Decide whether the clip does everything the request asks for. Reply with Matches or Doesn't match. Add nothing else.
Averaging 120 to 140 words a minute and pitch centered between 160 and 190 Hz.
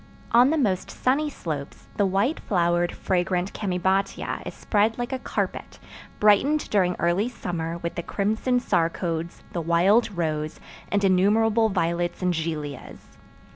Matches